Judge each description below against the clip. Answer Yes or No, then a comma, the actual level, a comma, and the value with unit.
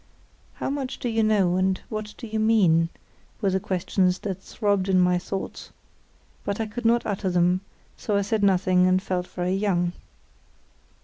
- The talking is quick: No, average, 175 wpm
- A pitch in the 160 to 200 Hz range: Yes, high, 190 Hz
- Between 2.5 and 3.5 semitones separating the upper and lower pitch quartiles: Yes, average, 2.8 semitones